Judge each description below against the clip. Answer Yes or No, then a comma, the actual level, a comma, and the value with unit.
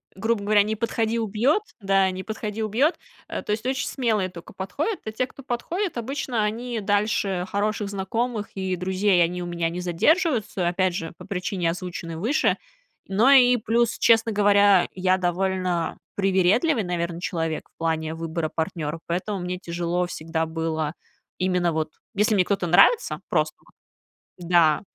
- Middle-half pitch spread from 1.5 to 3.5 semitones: No, average, 4.0 semitones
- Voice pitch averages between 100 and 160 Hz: No, high, 190 Hz